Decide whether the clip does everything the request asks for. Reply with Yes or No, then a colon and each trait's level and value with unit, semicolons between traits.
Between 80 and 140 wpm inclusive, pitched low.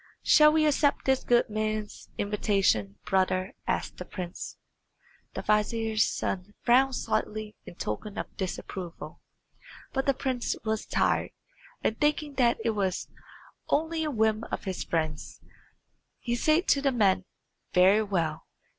No: slow, 135 wpm; high, 215 Hz